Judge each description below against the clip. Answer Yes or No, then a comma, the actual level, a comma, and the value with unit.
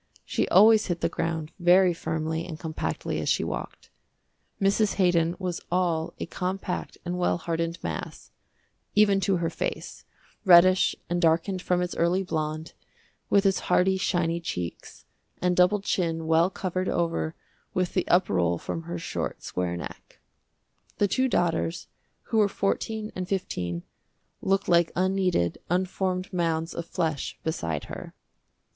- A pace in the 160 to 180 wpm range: No, average, 145 wpm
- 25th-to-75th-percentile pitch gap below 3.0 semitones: Yes, narrow, 2.4 semitones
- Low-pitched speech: No, medium, 175 Hz